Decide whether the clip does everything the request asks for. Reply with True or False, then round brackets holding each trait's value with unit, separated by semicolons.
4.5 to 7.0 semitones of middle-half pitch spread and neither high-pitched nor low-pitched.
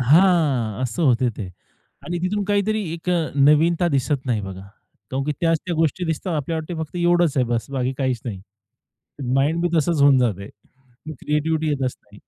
True (5.0 semitones; 150 Hz)